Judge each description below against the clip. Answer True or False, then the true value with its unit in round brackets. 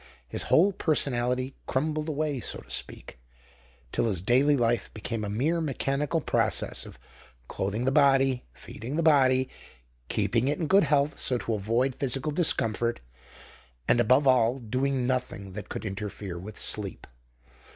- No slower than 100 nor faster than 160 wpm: True (150 wpm)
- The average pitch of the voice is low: True (130 Hz)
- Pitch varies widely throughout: False (4.1 semitones)